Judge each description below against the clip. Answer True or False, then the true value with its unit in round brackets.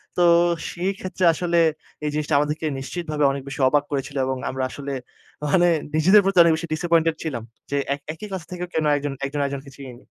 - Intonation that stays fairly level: False (3.6 semitones)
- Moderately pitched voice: True (155 Hz)